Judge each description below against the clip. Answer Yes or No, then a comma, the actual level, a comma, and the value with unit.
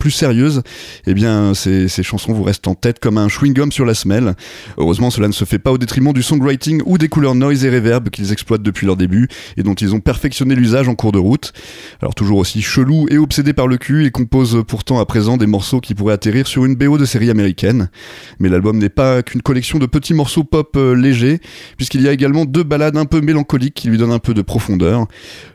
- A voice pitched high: No, low, 125 Hz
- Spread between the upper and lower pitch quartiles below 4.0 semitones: No, average, 4.8 semitones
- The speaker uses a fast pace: Yes, fast, 235 wpm